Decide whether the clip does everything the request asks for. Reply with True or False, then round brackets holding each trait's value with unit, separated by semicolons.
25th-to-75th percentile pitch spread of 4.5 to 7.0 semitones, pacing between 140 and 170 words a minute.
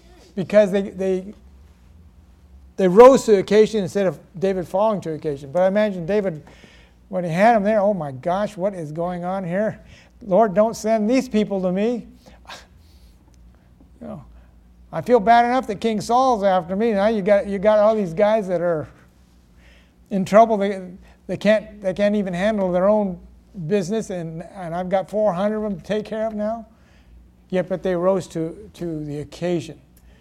False (5.2 semitones; 180 wpm)